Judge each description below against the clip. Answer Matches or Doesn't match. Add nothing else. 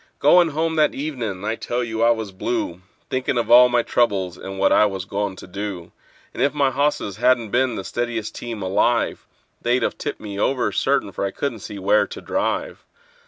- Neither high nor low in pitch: Doesn't match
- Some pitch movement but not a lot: Matches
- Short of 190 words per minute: Doesn't match